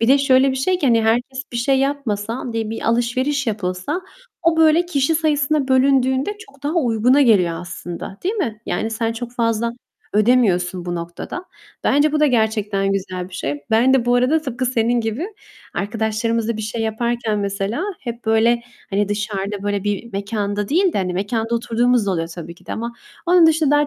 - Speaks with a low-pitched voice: No, high, 230 Hz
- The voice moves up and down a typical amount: Yes, average, 4.6 semitones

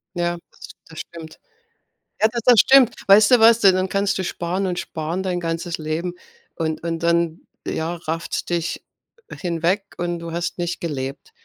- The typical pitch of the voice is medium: Yes, medium, 175 Hz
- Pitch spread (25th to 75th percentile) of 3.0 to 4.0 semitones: No, narrow, 2.4 semitones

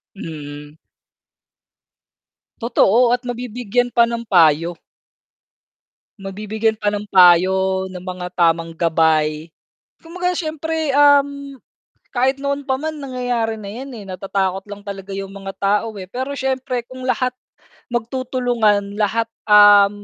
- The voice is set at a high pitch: Yes, high, 210 Hz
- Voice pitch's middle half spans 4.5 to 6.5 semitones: Yes, average, 5.1 semitones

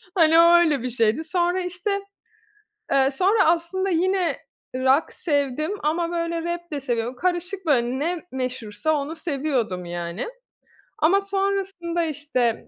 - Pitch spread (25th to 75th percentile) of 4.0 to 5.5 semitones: Yes, average, 5.2 semitones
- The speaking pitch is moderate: No, very high, 320 Hz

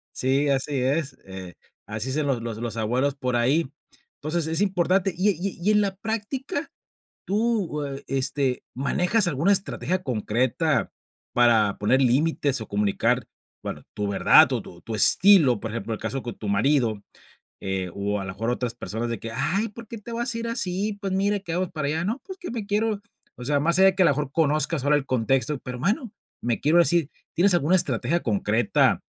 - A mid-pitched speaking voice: Yes, medium, 145 Hz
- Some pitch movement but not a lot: No, wide, 8.0 semitones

